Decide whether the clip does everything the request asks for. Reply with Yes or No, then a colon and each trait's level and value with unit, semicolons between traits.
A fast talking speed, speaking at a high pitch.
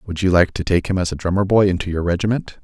No: fast, 295 wpm; very low, 90 Hz